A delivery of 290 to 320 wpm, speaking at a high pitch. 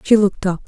No: fast, 270 wpm; high, 195 Hz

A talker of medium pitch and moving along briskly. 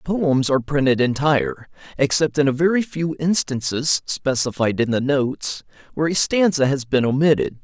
No: medium, 145 Hz; average, 165 wpm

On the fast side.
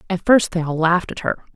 Yes: fast, 270 wpm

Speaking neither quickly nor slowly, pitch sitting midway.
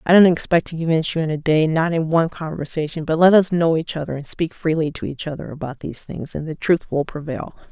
No: fast, 250 wpm; medium, 160 Hz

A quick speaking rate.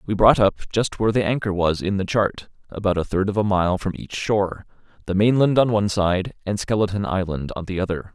Yes: fast, 230 wpm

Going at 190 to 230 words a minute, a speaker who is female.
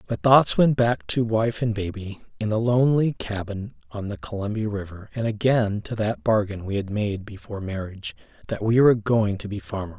No: average, 200 wpm; male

